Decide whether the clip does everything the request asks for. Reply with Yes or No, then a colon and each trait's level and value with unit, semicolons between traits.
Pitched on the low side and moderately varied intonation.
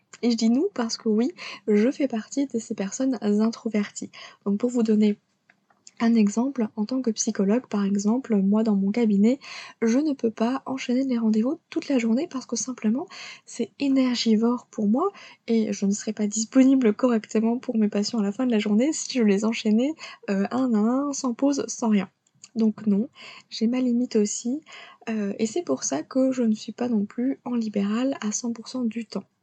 No: high, 230 Hz; average, 3.1 semitones